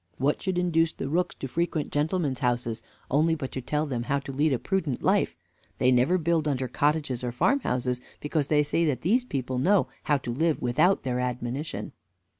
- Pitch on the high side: No, medium, 145 Hz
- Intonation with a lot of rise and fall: No, average, 4.4 semitones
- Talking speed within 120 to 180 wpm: No, average, 195 wpm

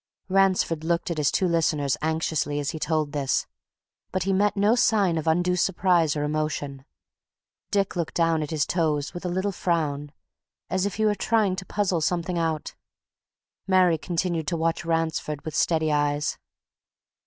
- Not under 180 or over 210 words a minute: No, average, 165 wpm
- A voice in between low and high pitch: Yes, medium, 165 Hz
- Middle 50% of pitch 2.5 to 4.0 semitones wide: Yes, average, 3.3 semitones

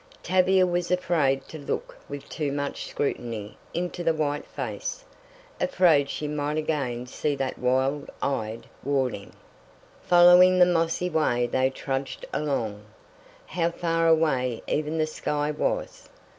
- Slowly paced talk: Yes, slow, 130 wpm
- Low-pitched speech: No, medium, 150 Hz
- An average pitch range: Yes, average, 4.1 semitones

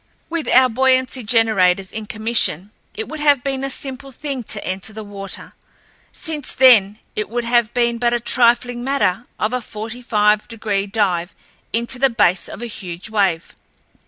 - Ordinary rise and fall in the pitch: Yes, average, 3.5 semitones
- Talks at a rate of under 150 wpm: No, average, 170 wpm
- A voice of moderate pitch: No, high, 230 Hz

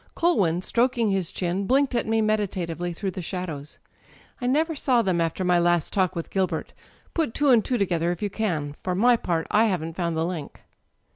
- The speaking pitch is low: No, medium, 185 Hz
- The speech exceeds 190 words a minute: Yes, average, 200 wpm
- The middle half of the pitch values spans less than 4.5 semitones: No, average, 4.9 semitones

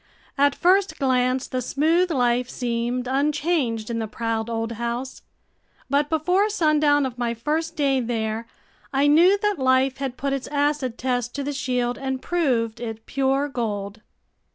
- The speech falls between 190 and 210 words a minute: No, average, 155 wpm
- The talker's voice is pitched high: Yes, very high, 260 Hz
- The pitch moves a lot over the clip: No, average, 3.6 semitones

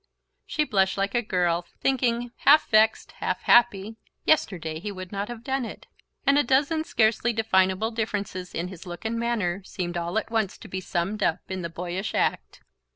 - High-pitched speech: Yes, high, 205 Hz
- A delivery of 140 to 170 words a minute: No, average, 185 wpm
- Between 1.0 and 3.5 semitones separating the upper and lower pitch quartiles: No, average, 4.3 semitones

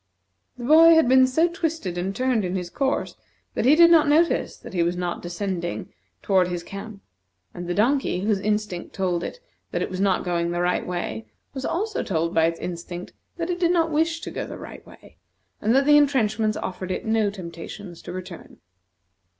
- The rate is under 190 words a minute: No, average, 200 wpm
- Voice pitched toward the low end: No, high, 200 Hz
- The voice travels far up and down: Yes, wide, 8.2 semitones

